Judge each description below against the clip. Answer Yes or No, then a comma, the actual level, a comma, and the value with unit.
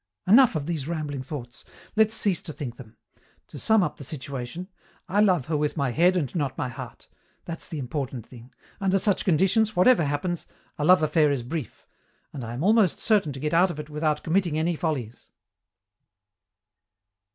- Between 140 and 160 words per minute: No, average, 185 wpm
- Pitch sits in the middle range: Yes, medium, 155 Hz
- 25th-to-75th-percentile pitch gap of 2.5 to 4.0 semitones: No, average, 4.8 semitones